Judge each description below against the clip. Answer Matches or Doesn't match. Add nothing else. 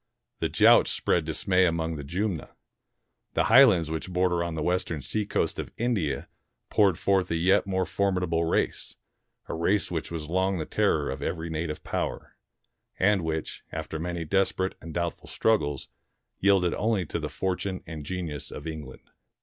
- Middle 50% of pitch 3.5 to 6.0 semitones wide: Doesn't match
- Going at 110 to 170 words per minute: Matches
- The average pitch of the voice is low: Matches